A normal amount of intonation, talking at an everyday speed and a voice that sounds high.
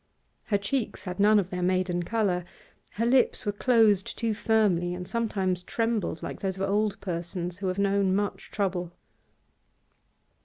Yes: average, 3.0 semitones; average, 155 wpm; high, 195 Hz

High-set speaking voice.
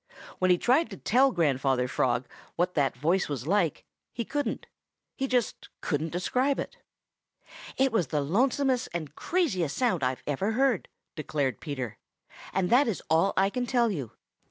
No: medium, 180 Hz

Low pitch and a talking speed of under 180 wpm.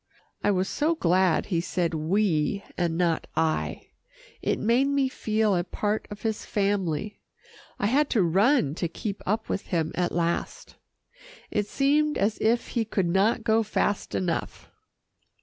No: high, 205 Hz; average, 155 wpm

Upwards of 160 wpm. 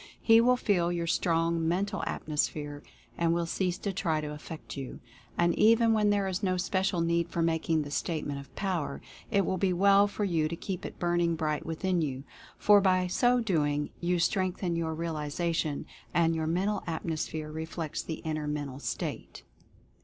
Yes: average, 175 wpm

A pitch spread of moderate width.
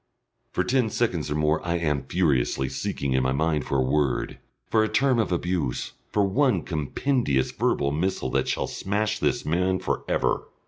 No: wide, 7.1 semitones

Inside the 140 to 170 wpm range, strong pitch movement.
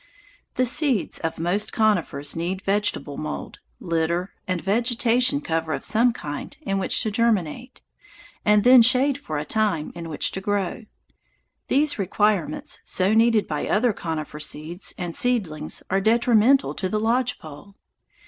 Yes: average, 150 wpm; wide, 6.0 semitones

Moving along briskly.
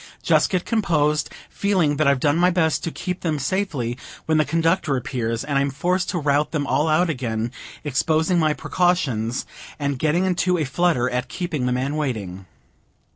No: average, 180 wpm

